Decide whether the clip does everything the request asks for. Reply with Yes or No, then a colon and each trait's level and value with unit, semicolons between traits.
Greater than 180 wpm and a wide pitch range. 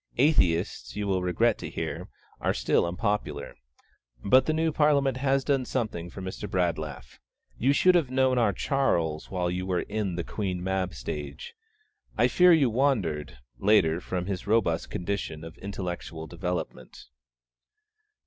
No: average, 150 wpm; wide, 6.8 semitones